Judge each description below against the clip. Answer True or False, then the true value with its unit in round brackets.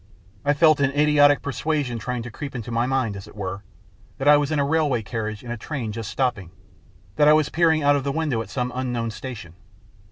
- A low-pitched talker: True (130 Hz)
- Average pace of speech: False (225 wpm)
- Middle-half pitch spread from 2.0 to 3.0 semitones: False (4.1 semitones)